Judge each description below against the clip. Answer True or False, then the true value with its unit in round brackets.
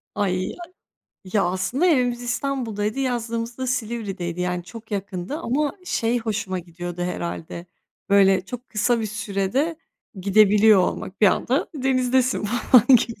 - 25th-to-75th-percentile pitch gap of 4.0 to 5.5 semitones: True (4.7 semitones)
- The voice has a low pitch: False (220 Hz)